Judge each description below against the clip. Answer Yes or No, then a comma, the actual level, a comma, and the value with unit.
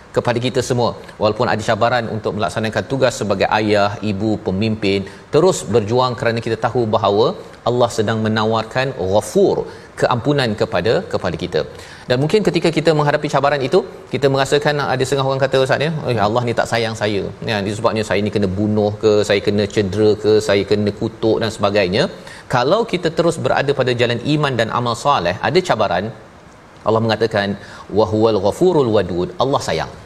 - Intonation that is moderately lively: Yes, average, 4.0 semitones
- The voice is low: Yes, low, 115 Hz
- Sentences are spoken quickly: Yes, fast, 165 wpm